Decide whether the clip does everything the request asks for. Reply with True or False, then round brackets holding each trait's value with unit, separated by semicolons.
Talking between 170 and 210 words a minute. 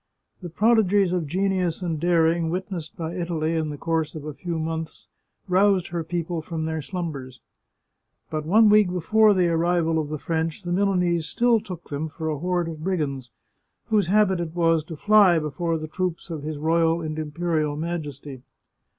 True (175 wpm)